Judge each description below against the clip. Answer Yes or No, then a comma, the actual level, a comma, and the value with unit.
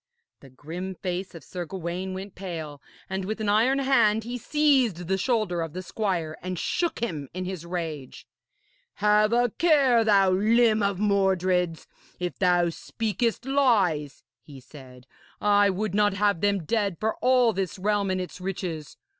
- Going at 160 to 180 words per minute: Yes, average, 165 wpm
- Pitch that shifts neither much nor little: Yes, average, 3.6 semitones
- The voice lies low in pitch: No, high, 190 Hz